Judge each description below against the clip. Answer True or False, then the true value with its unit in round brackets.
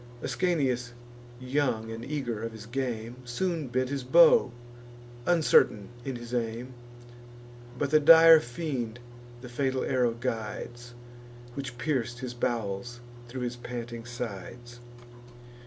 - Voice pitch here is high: False (120 Hz)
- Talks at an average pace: False (120 wpm)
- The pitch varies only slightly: True (2.3 semitones)